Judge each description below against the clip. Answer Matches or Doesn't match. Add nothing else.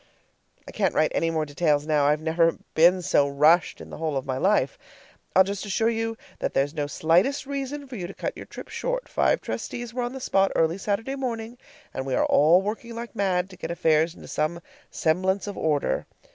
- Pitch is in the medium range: Matches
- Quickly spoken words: Matches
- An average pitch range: Doesn't match